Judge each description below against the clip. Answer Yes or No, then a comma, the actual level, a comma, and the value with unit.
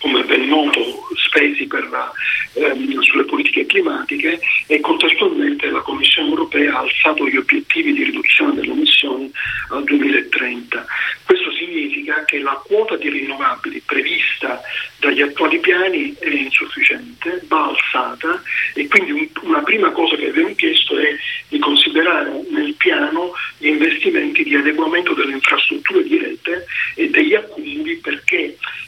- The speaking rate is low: No, average, 135 wpm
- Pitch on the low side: No, very high, 335 Hz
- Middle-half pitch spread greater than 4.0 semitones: No, average, 3.2 semitones